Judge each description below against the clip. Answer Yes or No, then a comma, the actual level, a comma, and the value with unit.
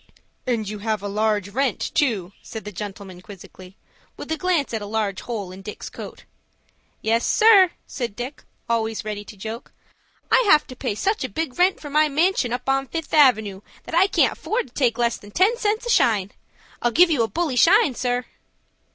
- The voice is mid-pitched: No, high, 240 Hz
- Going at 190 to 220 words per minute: Yes, average, 200 wpm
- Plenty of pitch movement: Yes, wide, 6.6 semitones